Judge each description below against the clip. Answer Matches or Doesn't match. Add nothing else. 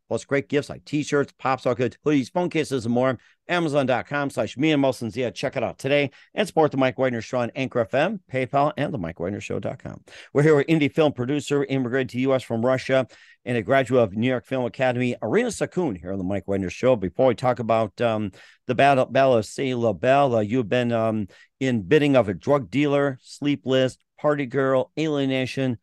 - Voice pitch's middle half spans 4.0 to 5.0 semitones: Doesn't match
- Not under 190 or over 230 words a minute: Matches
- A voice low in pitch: Matches